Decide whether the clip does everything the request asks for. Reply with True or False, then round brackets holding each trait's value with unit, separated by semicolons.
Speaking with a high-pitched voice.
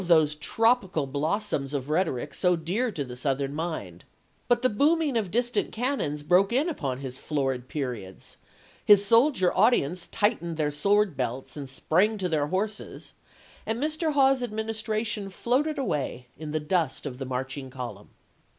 False (175 Hz)